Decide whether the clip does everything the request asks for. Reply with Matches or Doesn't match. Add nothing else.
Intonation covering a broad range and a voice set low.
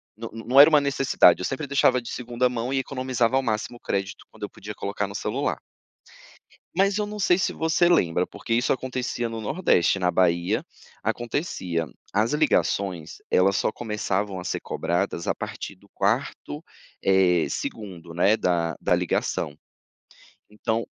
Matches